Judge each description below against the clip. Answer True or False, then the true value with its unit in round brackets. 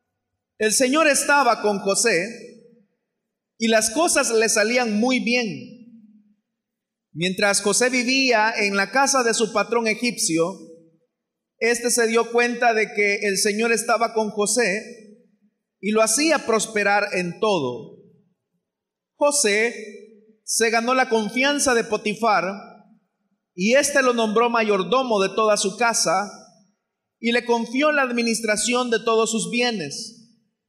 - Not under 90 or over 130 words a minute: True (125 wpm)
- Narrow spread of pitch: True (2.3 semitones)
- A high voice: True (225 Hz)